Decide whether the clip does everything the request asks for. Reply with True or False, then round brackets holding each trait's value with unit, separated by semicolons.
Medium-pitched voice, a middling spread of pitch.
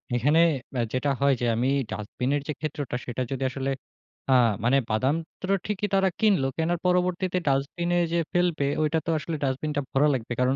True (145 Hz; 4.7 semitones)